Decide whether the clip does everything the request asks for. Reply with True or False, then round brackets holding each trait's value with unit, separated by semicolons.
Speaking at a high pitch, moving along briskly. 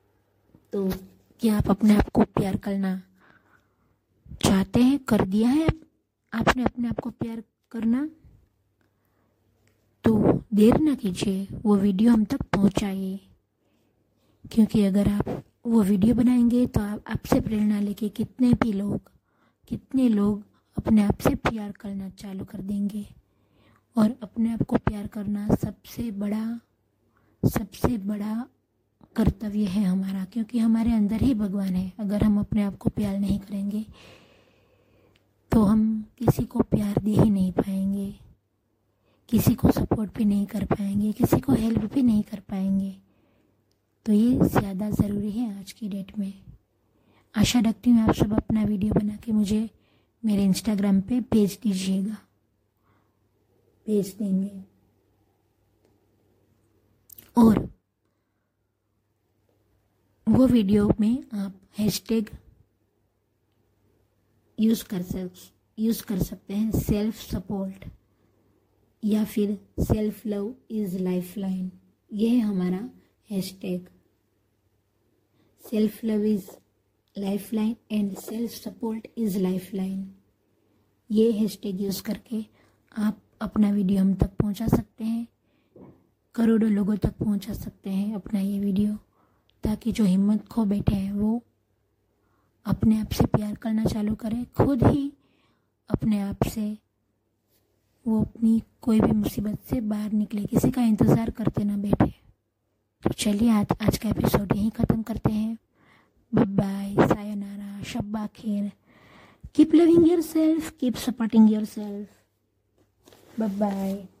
False (205 Hz; 125 wpm)